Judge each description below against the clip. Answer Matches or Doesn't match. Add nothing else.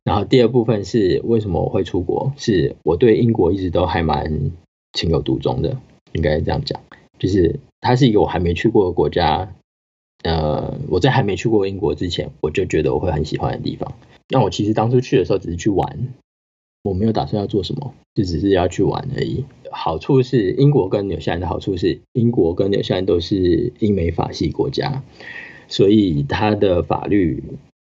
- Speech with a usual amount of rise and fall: Doesn't match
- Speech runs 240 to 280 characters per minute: Doesn't match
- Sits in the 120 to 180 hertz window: Doesn't match